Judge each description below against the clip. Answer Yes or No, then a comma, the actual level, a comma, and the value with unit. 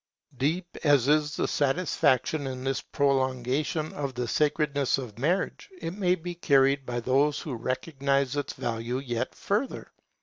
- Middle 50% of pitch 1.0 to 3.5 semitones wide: Yes, average, 3.0 semitones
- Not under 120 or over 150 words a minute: Yes, average, 145 wpm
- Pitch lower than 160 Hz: Yes, medium, 140 Hz